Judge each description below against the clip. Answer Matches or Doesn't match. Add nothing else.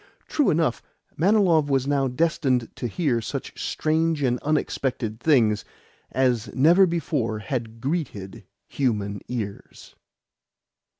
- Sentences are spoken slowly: Matches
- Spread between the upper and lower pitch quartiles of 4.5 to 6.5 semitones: Matches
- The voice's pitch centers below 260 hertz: Matches